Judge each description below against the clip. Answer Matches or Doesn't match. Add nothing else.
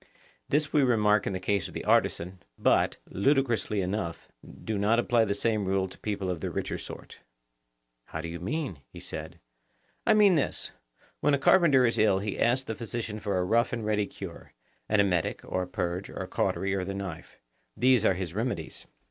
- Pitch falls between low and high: Doesn't match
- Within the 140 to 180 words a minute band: Doesn't match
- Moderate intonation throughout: Matches